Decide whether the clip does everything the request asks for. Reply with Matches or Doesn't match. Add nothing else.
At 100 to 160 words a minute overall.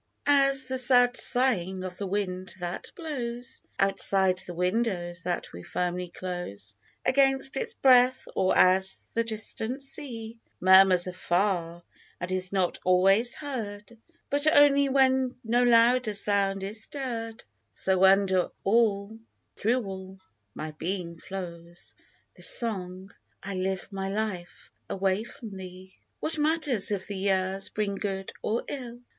Matches